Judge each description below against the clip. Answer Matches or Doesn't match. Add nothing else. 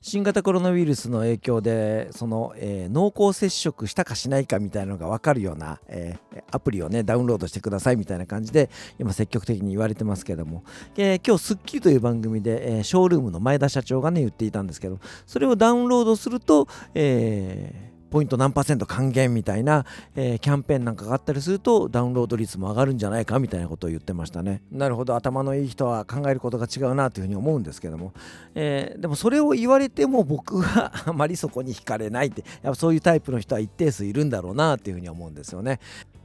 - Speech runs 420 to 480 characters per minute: Matches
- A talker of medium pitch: Doesn't match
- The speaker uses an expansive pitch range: Matches